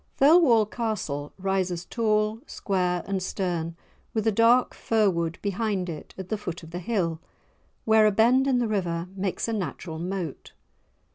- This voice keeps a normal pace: Yes, average, 160 wpm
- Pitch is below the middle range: No, high, 195 Hz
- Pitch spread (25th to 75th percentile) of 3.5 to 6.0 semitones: Yes, average, 4.1 semitones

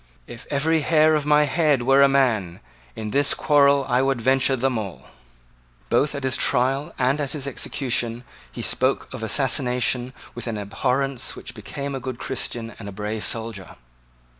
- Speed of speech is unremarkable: Yes, average, 170 wpm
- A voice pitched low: Yes, low, 130 Hz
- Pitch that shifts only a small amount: No, average, 3.0 semitones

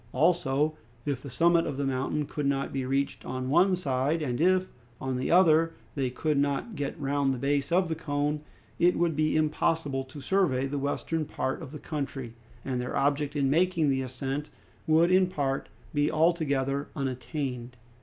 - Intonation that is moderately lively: Yes, average, 3.1 semitones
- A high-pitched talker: No, medium, 145 Hz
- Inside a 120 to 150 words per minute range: No, average, 180 wpm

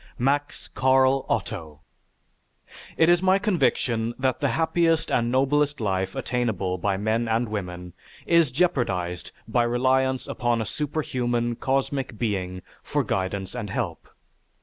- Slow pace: Yes, slow, 125 wpm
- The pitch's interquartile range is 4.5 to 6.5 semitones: Yes, average, 5.2 semitones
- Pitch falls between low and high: No, low, 120 Hz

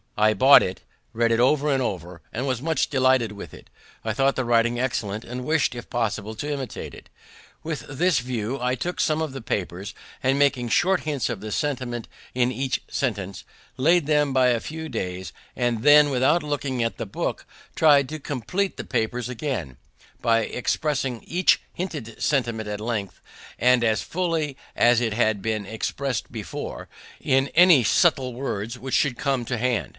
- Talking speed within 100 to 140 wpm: No, average, 180 wpm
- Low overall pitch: Yes, low, 125 Hz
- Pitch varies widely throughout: No, average, 4.1 semitones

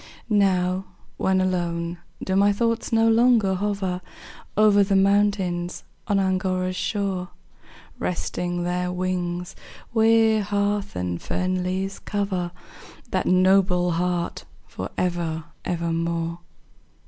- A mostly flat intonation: Yes, narrow, 2.3 semitones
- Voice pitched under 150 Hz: No, medium, 185 Hz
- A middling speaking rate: No, slow, 110 wpm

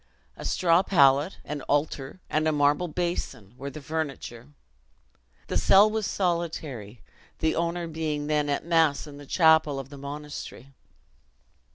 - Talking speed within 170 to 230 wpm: No, average, 145 wpm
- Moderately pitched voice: Yes, medium, 150 Hz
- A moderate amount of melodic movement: Yes, average, 3.1 semitones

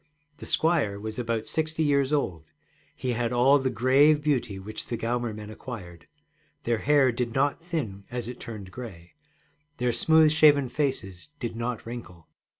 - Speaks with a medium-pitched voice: No, low, 120 Hz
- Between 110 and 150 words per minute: No, average, 160 wpm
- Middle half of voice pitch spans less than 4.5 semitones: No, average, 4.8 semitones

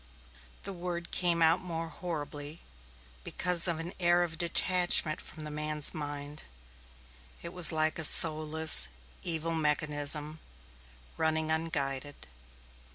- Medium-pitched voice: Yes, medium, 160 Hz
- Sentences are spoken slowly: Yes, slow, 110 wpm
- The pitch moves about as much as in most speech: No, narrow, 2.1 semitones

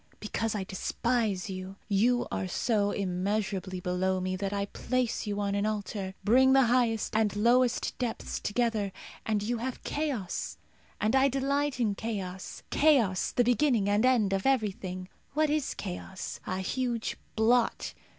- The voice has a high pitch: Yes, high, 215 Hz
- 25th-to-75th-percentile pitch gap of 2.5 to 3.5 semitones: No, average, 4.2 semitones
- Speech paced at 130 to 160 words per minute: Yes, average, 150 wpm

